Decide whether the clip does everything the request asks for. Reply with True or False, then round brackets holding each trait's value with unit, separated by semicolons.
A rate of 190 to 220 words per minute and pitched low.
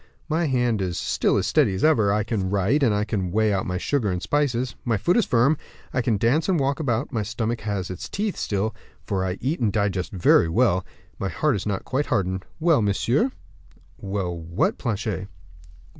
True (200 wpm; 110 Hz)